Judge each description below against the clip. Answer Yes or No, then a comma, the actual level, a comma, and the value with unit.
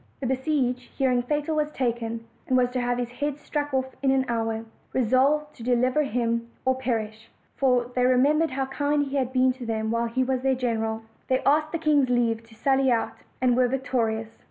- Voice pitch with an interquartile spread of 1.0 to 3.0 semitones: Yes, narrow, 2.4 semitones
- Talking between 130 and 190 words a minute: No, fast, 205 wpm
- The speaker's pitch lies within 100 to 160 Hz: No, very high, 255 Hz